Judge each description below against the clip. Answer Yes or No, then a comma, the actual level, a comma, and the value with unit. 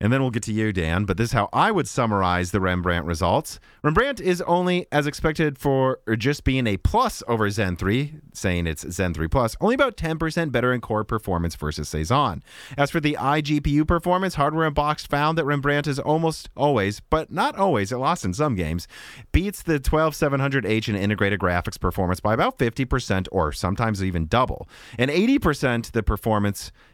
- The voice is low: Yes, low, 125 Hz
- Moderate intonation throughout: No, wide, 7.3 semitones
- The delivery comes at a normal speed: Yes, average, 185 wpm